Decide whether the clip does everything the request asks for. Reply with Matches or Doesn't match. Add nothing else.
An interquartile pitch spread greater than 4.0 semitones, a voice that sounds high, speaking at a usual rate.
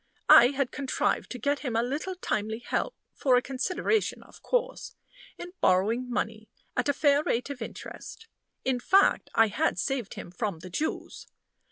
Matches